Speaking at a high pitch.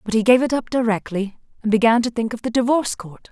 Yes: high, 230 Hz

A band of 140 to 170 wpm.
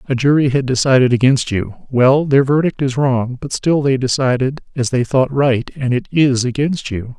No: average, 200 wpm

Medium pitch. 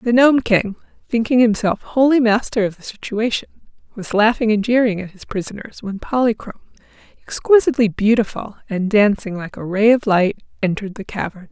No: high, 220 Hz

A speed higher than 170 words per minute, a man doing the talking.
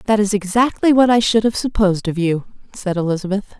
No: average, 200 wpm; female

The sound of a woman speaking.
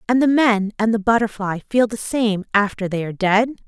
Yes: female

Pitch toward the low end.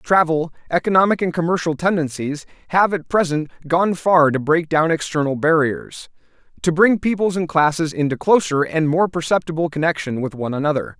No: medium, 165 Hz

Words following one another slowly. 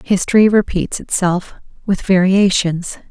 Yes: slow, 75 wpm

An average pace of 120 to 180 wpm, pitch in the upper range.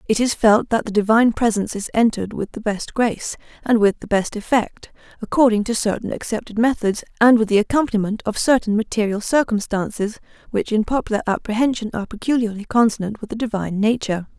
Yes: average, 175 wpm; high, 220 Hz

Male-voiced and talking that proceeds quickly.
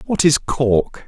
No: male; average, 170 wpm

